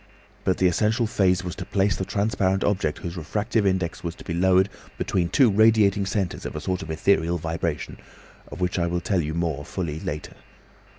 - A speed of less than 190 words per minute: No, average, 195 wpm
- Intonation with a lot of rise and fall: No, average, 2.9 semitones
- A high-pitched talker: No, very low, 90 Hz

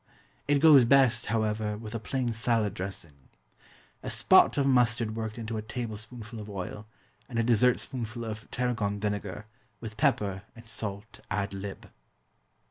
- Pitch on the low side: Yes, low, 110 Hz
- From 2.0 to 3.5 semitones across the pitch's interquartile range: Yes, narrow, 2.4 semitones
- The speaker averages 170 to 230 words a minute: No, average, 150 wpm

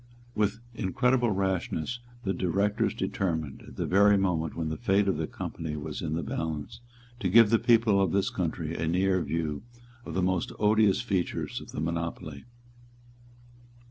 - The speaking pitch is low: Yes, very low, 95 Hz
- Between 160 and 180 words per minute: Yes, average, 165 wpm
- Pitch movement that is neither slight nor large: Yes, average, 4.2 semitones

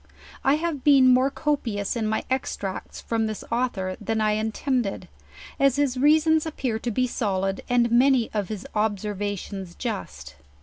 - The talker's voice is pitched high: Yes, high, 235 Hz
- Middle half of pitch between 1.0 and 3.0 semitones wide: No, average, 4.3 semitones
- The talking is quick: No, average, 155 wpm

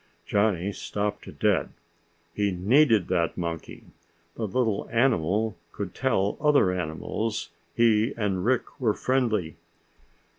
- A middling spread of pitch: Yes, average, 4.1 semitones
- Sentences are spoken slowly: Yes, slow, 110 wpm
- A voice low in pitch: Yes, low, 105 Hz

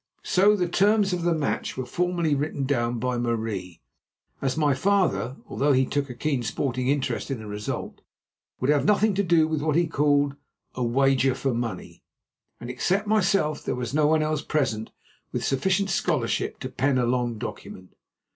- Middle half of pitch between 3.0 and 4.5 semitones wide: No, average, 5.2 semitones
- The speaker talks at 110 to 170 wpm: No, average, 180 wpm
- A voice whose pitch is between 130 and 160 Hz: Yes, medium, 140 Hz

